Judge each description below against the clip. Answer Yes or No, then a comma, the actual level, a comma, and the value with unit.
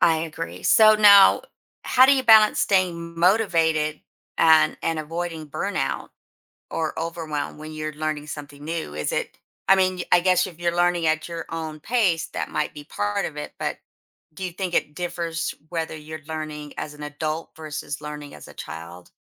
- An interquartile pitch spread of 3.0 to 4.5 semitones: No, narrow, 2.5 semitones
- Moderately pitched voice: Yes, medium, 160 Hz